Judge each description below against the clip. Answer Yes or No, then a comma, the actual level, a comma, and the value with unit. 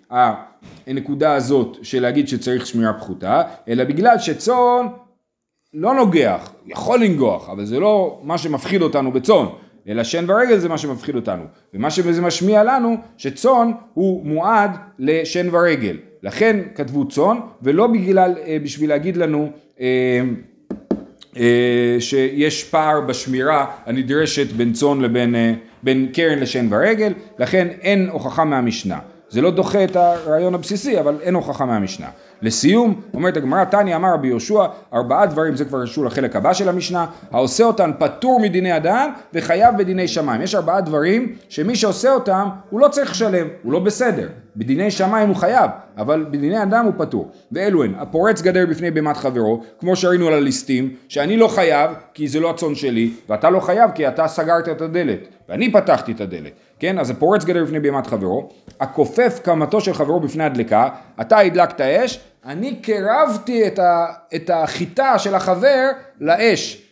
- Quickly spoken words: Yes, fast, 155 wpm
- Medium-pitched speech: Yes, medium, 170 Hz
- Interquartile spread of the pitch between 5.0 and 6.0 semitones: No, wide, 6.4 semitones